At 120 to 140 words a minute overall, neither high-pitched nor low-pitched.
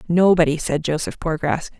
Yes: slow, 135 wpm; medium, 160 Hz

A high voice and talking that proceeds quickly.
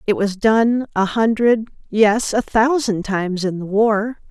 No: high, 215 Hz; average, 165 wpm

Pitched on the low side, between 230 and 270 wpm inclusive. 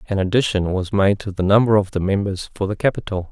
Yes: low, 100 Hz; fast, 235 wpm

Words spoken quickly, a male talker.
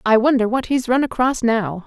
No: fast, 225 wpm; female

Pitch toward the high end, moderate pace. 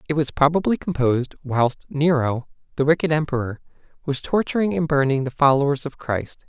No: medium, 145 Hz; average, 155 wpm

